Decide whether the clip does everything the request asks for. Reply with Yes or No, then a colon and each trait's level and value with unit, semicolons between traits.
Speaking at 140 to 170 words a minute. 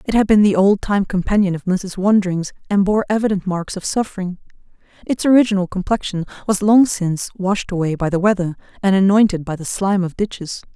No: average, 190 wpm